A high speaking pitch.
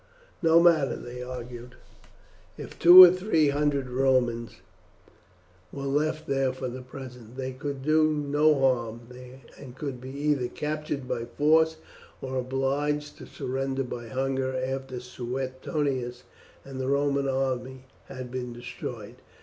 No: low, 135 Hz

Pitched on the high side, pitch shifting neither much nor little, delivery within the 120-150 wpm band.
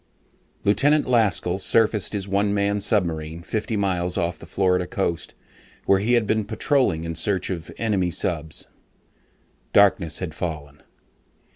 No: very low, 95 Hz; average, 3.6 semitones; average, 140 wpm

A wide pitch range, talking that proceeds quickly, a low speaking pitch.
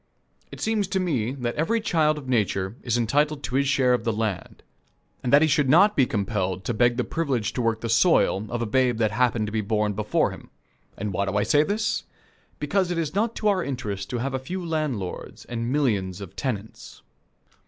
Yes: wide, 6.0 semitones; fast, 215 wpm; low, 125 Hz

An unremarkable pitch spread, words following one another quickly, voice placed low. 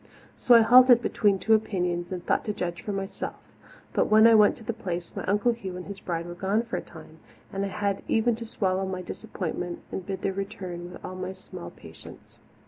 No: average, 3.2 semitones; fast, 220 wpm; high, 195 Hz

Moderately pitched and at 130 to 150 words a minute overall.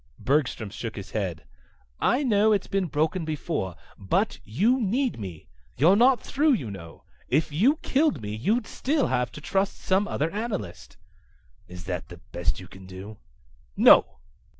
No: medium, 150 Hz; average, 160 wpm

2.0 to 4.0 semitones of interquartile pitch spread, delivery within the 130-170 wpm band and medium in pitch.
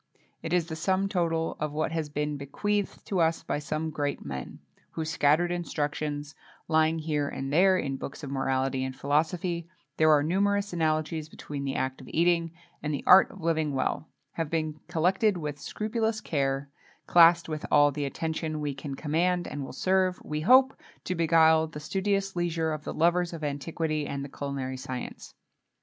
No: average, 3.1 semitones; average, 180 wpm; medium, 160 Hz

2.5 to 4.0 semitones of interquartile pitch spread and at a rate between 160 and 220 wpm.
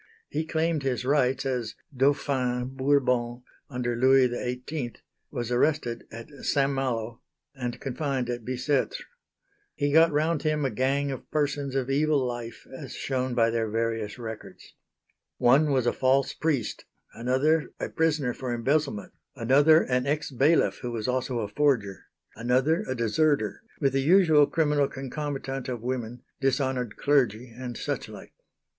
No: average, 3.0 semitones; average, 145 wpm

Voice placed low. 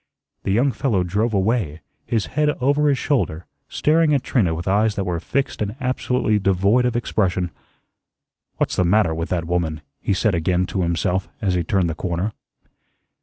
Yes: low, 100 Hz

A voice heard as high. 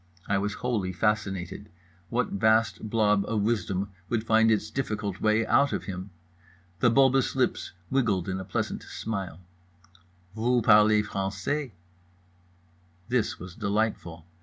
No: low, 105 Hz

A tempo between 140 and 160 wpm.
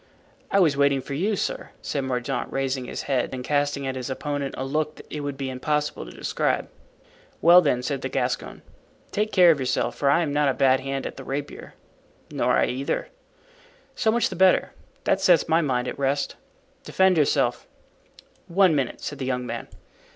No: average, 190 wpm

